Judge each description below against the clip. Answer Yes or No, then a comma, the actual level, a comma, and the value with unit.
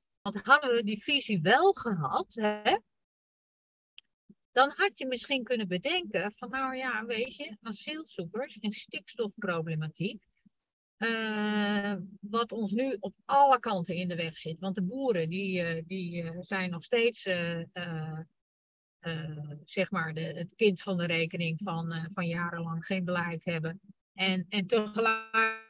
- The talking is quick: No, average, 145 wpm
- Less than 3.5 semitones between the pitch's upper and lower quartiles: No, average, 4.9 semitones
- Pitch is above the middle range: Yes, high, 195 Hz